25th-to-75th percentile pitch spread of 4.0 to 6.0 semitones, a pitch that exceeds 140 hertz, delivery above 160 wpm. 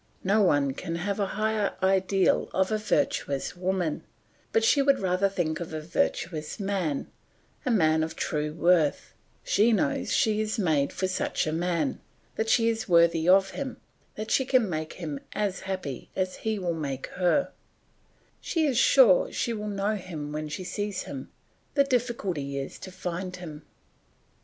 Yes: average, 5.2 semitones; medium, 185 Hz; average, 170 wpm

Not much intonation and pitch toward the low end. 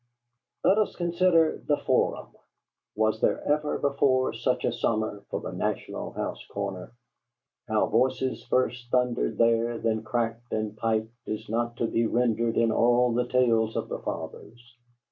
Yes: narrow, 2.3 semitones; low, 120 Hz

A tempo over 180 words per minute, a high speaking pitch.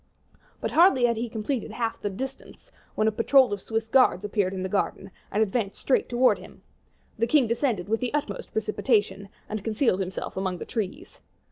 Yes: average, 190 wpm; high, 220 Hz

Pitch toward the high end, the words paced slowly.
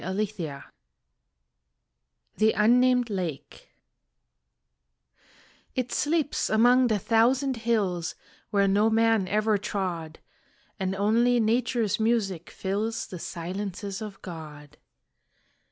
Yes: high, 210 Hz; slow, 90 wpm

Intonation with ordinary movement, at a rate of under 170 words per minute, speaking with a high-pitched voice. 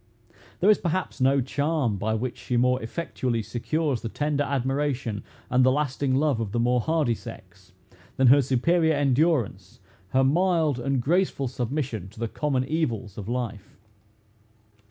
No: average, 3.8 semitones; average, 155 wpm; low, 130 Hz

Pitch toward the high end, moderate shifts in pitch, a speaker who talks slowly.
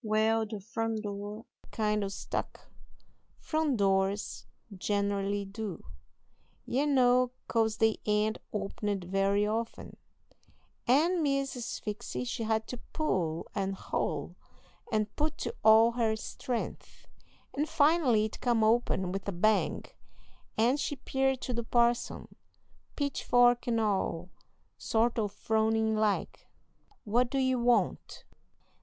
Yes: high, 220 Hz; average, 3.1 semitones; slow, 125 wpm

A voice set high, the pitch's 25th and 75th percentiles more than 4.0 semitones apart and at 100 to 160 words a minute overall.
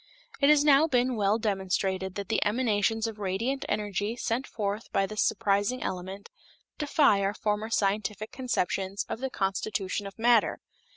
No: high, 210 Hz; average, 3.2 semitones; average, 155 wpm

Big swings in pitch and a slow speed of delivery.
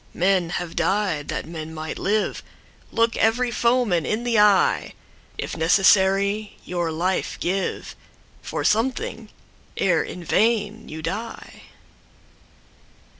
No: average, 4.5 semitones; slow, 100 wpm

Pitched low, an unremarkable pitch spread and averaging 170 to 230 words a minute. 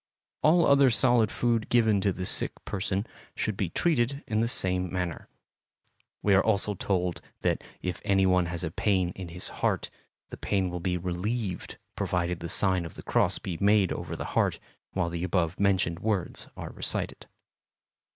Yes: very low, 95 Hz; average, 3.3 semitones; average, 175 wpm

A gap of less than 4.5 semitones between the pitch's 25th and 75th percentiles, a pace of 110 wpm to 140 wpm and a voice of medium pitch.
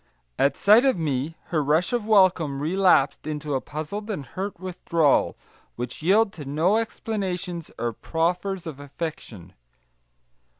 No: average, 5.0 semitones; slow, 135 wpm; medium, 170 Hz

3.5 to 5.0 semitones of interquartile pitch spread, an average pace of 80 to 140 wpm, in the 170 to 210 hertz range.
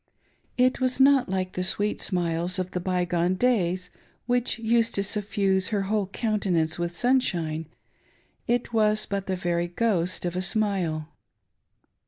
No: average, 3.9 semitones; average, 155 wpm; high, 190 Hz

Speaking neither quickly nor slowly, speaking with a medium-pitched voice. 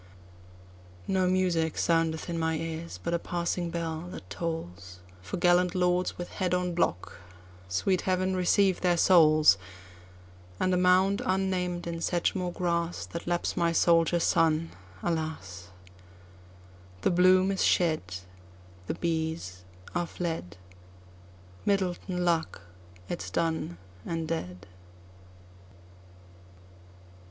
No: slow, 100 wpm; medium, 165 Hz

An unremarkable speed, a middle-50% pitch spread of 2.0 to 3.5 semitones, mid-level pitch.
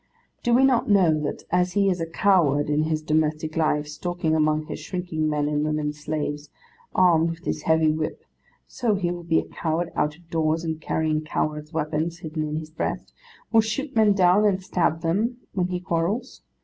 Yes: average, 195 wpm; average, 2.8 semitones; medium, 160 Hz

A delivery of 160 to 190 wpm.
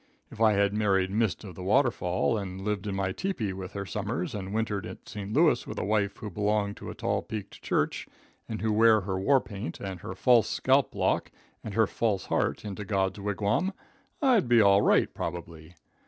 No: fast, 205 wpm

